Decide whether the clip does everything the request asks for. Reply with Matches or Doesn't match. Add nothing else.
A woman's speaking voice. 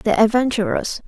Matches